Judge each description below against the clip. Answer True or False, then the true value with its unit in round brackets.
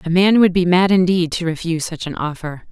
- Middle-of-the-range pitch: True (175 Hz)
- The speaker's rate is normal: False (245 wpm)